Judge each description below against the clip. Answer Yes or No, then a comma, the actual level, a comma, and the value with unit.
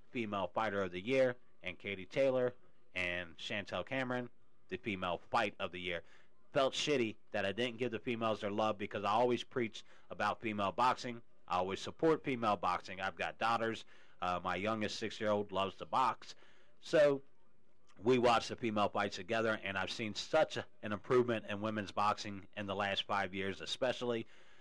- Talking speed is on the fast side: No, average, 180 wpm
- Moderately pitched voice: No, low, 110 Hz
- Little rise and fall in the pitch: No, average, 3.4 semitones